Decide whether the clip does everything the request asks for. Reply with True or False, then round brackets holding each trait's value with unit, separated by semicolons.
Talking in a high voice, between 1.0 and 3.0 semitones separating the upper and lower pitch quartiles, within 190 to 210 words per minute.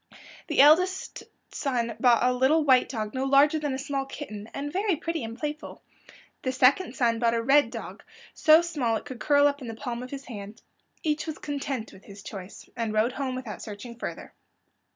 False (260 Hz; 4.1 semitones; 200 wpm)